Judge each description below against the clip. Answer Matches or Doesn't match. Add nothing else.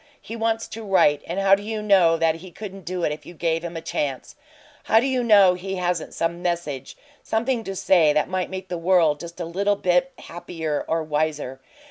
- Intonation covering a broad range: Doesn't match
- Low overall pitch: Doesn't match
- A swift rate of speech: Matches